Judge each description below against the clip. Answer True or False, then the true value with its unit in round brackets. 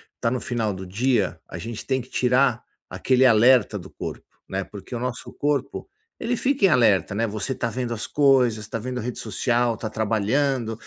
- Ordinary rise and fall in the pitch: True (3.0 semitones)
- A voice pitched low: True (120 Hz)